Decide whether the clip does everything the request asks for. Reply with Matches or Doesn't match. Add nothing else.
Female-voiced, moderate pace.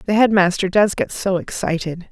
Matches